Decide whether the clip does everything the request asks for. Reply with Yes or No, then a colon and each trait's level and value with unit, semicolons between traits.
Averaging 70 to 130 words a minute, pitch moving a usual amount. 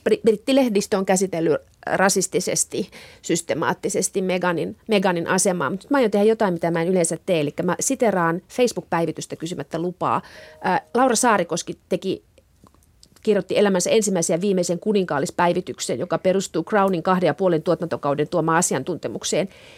Yes: average, 125 wpm; average, 3.5 semitones